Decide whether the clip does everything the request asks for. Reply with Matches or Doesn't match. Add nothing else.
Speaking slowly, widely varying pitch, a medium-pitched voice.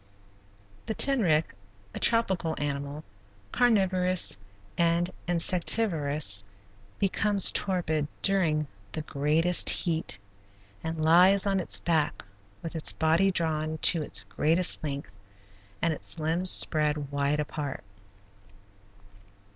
Doesn't match